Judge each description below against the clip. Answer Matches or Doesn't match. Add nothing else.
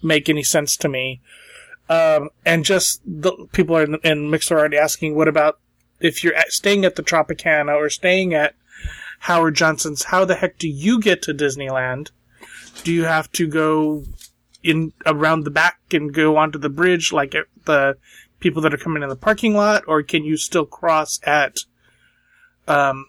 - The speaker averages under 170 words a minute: Doesn't match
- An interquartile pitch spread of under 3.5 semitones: Matches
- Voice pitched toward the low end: Doesn't match